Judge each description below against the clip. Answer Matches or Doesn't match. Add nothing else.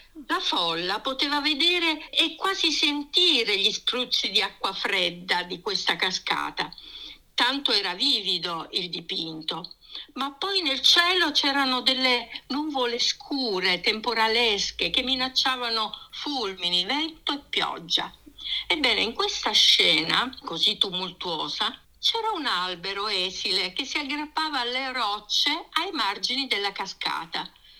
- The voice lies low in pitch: Doesn't match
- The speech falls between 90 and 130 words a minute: Matches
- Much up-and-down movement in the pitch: Matches